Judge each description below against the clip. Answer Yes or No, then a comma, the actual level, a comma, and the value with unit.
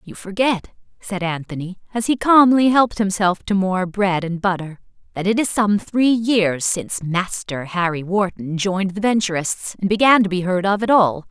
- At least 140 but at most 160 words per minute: No, average, 185 wpm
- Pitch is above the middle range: Yes, high, 195 Hz